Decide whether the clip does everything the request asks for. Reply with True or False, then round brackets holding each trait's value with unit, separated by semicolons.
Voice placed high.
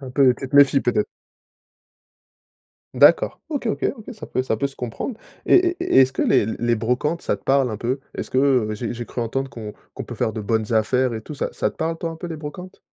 False (130 Hz)